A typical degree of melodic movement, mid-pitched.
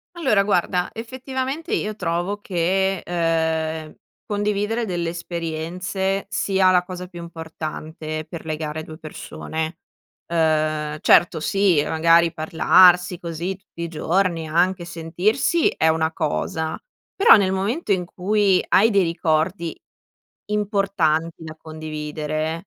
Yes: average, 3.5 semitones; medium, 170 Hz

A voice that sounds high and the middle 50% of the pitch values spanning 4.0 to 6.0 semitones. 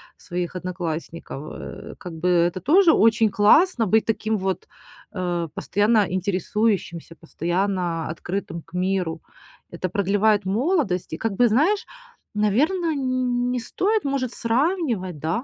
Yes: high, 205 Hz; wide, 5.5 semitones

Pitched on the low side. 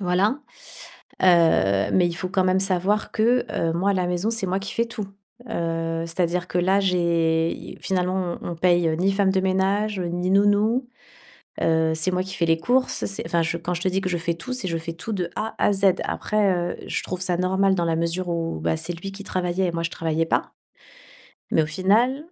No: medium, 180 Hz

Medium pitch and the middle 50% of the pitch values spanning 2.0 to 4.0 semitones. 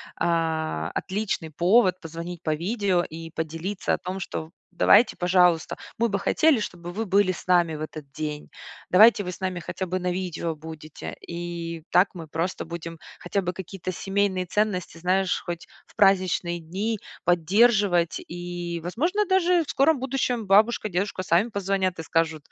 Yes: medium, 180 Hz; average, 3.2 semitones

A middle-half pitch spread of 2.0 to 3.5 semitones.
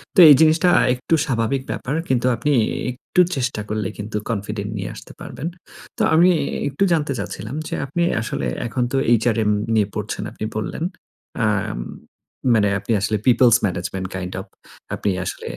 No: average, 4.6 semitones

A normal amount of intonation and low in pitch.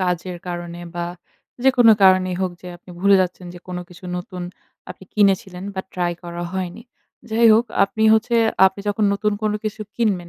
No: average, 3.0 semitones; medium, 185 Hz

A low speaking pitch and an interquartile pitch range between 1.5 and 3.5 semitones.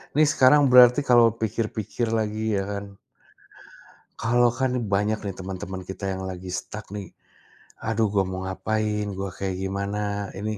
Yes: low, 105 Hz; average, 2.9 semitones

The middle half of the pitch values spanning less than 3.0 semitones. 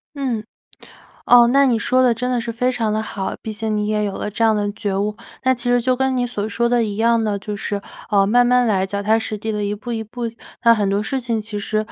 Yes: narrow, 2.6 semitones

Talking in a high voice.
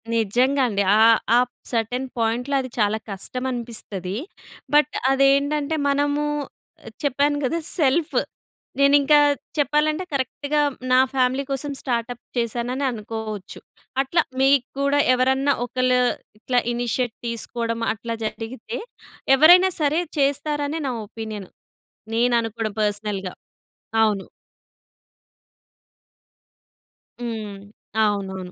Yes: very high, 250 Hz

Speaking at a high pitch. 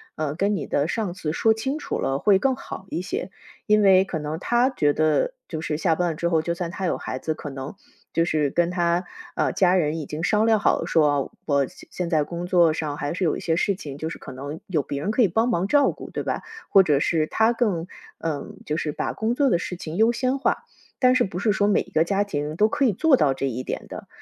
No: medium, 170 Hz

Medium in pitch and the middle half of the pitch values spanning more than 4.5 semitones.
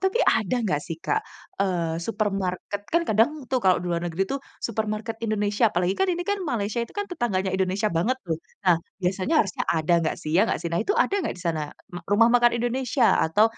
No: high, 205 Hz; average, 5.0 semitones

